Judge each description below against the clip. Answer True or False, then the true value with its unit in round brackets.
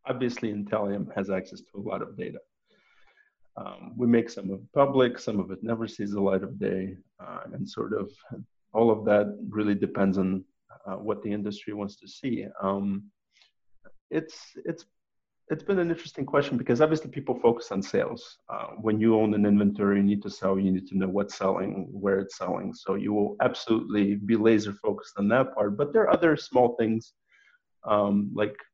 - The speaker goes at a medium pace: True (195 wpm)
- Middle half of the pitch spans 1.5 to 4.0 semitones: True (2.9 semitones)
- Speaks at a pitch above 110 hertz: False (105 Hz)